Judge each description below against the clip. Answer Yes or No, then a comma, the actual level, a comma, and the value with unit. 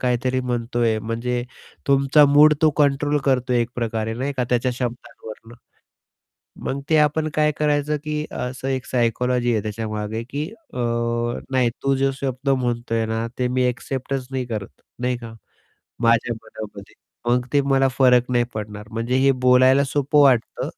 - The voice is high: No, low, 125 Hz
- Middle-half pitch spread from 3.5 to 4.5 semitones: No, average, 2.8 semitones